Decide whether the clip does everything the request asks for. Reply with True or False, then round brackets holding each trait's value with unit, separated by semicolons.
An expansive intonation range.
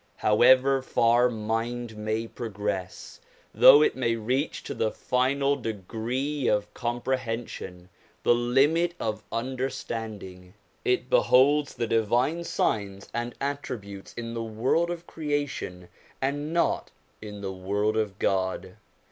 False (4.0 semitones)